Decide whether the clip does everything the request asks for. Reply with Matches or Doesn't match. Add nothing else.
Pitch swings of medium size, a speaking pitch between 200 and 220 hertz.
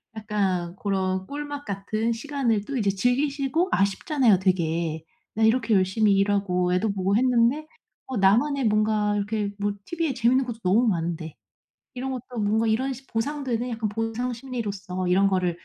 Matches